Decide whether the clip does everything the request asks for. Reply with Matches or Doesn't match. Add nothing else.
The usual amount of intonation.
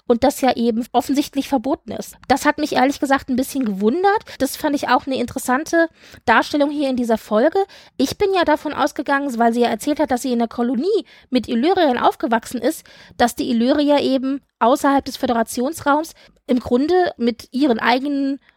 Matches